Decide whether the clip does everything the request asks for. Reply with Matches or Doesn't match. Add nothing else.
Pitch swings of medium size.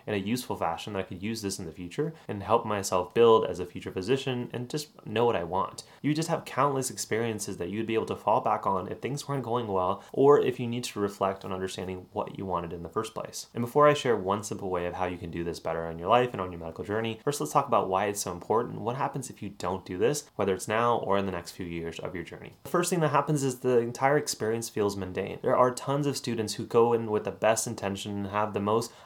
Matches